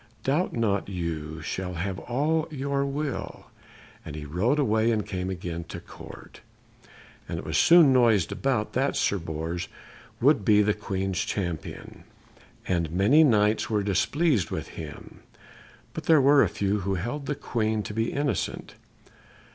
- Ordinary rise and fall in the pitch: No, wide, 6.9 semitones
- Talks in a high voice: No, low, 105 Hz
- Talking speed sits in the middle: Yes, average, 155 wpm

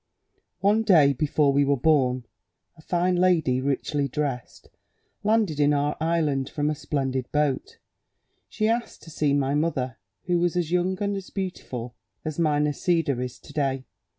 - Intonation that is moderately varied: Yes, average, 4.2 semitones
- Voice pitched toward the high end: No, medium, 150 Hz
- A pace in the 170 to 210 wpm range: No, average, 155 wpm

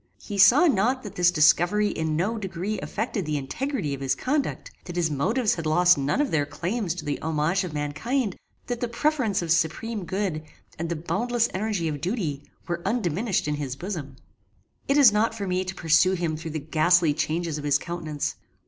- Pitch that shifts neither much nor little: No, wide, 5.7 semitones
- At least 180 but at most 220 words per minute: Yes, average, 195 wpm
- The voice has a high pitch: No, medium, 175 Hz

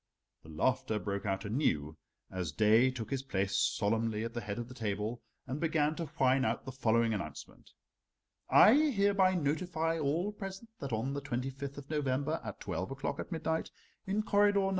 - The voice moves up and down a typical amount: No, wide, 6.7 semitones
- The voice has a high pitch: No, low, 130 Hz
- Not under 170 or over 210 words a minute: Yes, average, 180 wpm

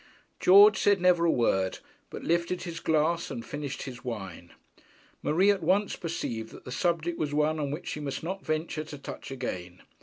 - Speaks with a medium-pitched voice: Yes, medium, 155 Hz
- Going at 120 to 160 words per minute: No, average, 185 wpm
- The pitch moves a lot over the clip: No, average, 5.0 semitones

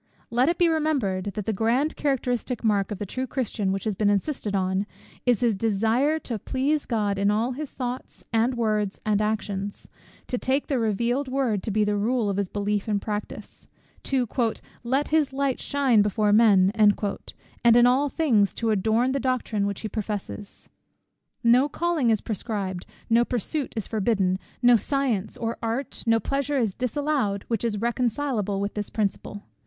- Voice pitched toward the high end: Yes, high, 225 Hz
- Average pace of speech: Yes, average, 175 wpm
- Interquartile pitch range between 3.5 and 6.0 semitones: Yes, average, 4.0 semitones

